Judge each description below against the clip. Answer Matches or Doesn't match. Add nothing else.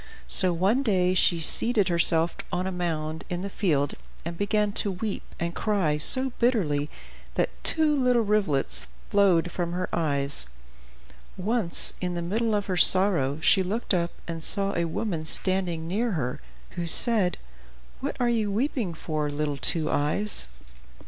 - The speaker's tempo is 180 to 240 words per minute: Doesn't match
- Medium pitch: Matches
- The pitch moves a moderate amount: Matches